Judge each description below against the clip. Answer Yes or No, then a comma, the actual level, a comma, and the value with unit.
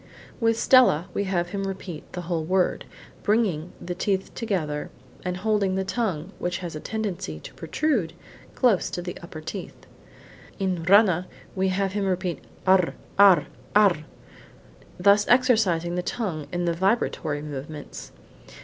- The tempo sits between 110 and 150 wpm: Yes, average, 145 wpm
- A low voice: No, medium, 185 Hz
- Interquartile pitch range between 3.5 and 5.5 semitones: No, average, 3.0 semitones